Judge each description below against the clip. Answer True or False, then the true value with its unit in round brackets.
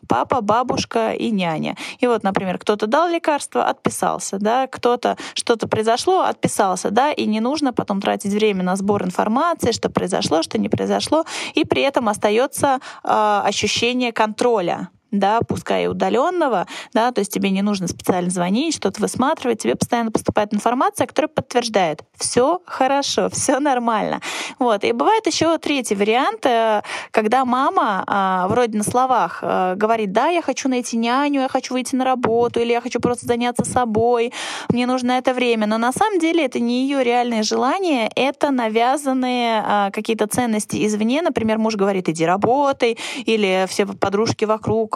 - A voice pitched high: True (235 Hz)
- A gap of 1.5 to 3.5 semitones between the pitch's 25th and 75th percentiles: False (3.9 semitones)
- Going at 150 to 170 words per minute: True (155 wpm)